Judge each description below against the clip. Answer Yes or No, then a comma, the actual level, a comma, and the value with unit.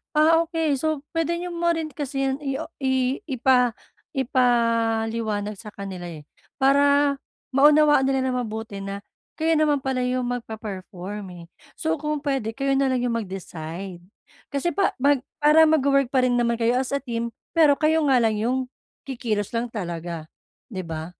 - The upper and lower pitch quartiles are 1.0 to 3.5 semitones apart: No, average, 4.5 semitones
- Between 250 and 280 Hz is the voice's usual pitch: Yes, very high, 255 Hz